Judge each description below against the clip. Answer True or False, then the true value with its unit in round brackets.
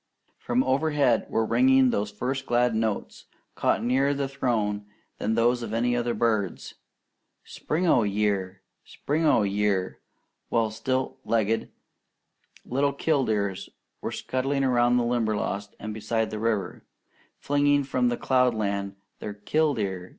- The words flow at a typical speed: False (130 wpm)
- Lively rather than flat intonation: False (4.1 semitones)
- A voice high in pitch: False (115 Hz)